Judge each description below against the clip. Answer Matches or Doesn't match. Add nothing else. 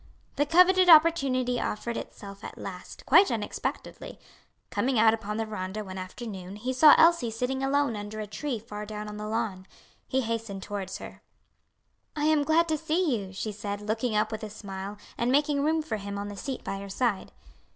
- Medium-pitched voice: Doesn't match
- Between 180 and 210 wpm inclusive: Matches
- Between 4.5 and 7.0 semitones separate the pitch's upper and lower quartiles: Matches